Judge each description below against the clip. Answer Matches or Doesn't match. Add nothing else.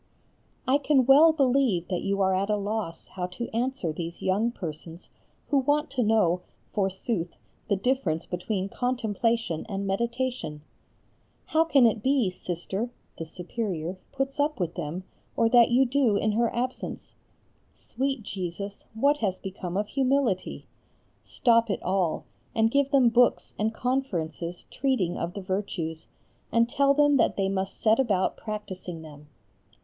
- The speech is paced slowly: Doesn't match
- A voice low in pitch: Doesn't match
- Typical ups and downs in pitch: Doesn't match